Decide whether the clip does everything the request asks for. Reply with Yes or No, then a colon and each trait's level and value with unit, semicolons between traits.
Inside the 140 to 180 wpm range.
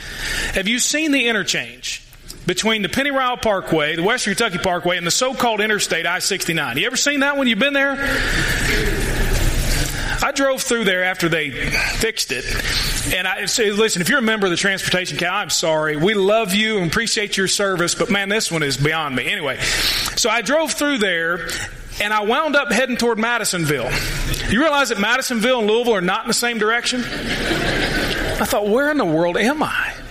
No: average, 195 wpm